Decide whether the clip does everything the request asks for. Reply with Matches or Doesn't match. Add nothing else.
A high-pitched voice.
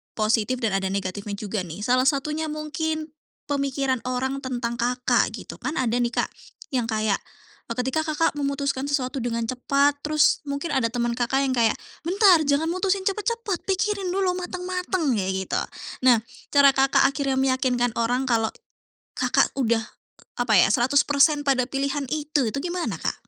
Matches